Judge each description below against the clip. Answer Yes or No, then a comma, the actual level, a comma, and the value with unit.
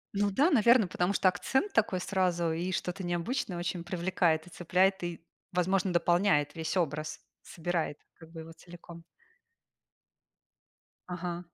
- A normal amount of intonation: No, narrow, 2.1 semitones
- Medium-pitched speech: Yes, medium, 175 Hz